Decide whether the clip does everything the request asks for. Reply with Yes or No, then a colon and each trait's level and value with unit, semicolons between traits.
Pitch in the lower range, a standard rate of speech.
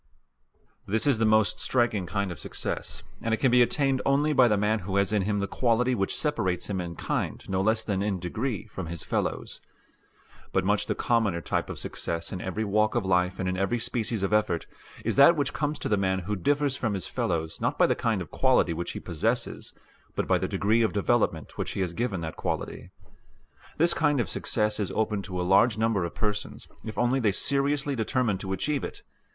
No: low, 105 Hz; fast, 220 wpm